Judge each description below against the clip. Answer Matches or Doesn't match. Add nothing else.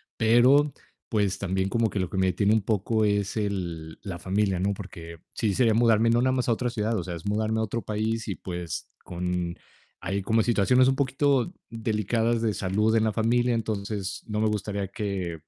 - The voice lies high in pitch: Doesn't match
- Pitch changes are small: Doesn't match